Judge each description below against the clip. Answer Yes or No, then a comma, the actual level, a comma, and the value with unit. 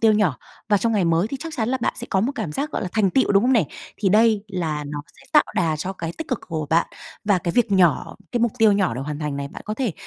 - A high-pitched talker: Yes, high, 200 Hz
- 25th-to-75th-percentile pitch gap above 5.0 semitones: Yes, wide, 5.6 semitones